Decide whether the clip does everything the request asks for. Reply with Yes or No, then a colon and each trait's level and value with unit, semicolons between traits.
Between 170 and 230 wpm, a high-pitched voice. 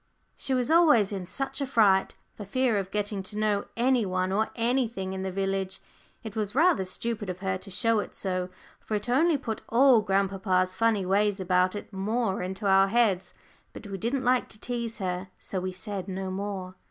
Yes: average, 200 wpm; high, 205 Hz